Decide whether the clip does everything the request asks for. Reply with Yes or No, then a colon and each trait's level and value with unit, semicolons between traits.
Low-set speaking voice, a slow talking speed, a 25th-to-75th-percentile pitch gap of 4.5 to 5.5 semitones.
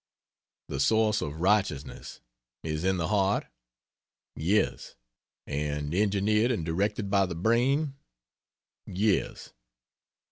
Yes: very low, 95 Hz; slow, 100 wpm; average, 5.0 semitones